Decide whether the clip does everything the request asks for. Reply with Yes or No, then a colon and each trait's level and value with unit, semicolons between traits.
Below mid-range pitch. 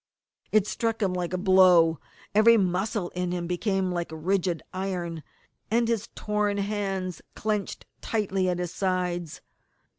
No: medium, 185 Hz